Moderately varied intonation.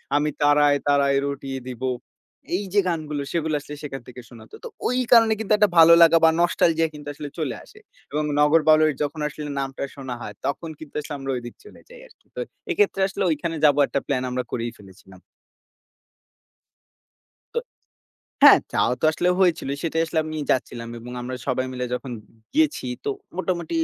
Yes: average, 3.8 semitones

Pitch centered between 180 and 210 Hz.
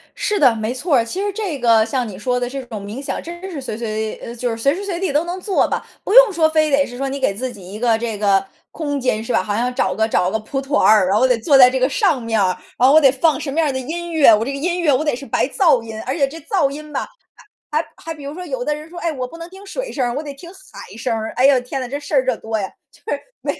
No: very high, 270 Hz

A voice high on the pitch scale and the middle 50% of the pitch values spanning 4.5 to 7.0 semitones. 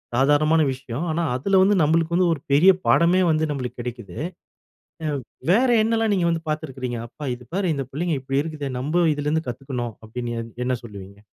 No: medium, 150 Hz; average, 5.0 semitones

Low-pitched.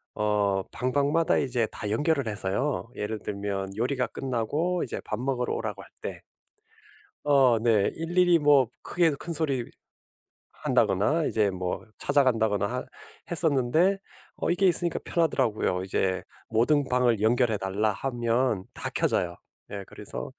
Yes: low, 120 Hz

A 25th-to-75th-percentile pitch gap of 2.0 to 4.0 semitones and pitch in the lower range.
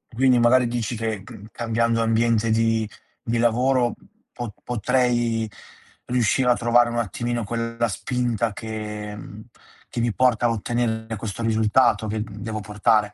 No: narrow, 1.6 semitones; low, 115 Hz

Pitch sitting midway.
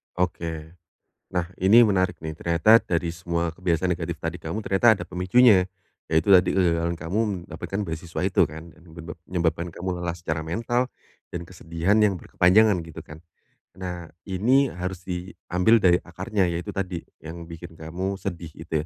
No: very low, 90 Hz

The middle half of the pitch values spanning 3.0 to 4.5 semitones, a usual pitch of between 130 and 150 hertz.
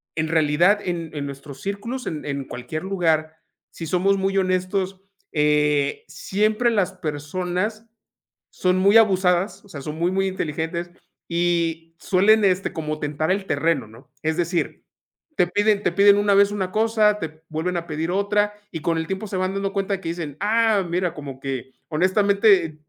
No: average, 4.0 semitones; medium, 180 Hz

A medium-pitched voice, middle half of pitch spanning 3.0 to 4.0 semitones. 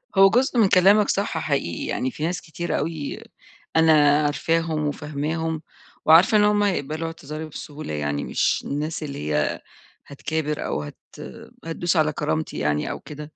No: medium, 155 Hz; narrow, 2.4 semitones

